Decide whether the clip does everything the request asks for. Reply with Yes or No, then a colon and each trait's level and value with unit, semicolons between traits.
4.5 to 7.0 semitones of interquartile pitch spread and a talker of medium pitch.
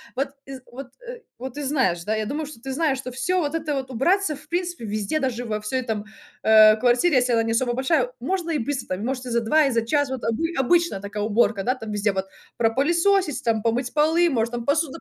No: average, 4.9 semitones; very high, 255 Hz